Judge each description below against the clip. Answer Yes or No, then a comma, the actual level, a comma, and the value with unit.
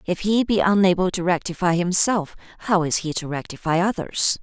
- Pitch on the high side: No, medium, 180 Hz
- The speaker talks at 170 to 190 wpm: Yes, average, 175 wpm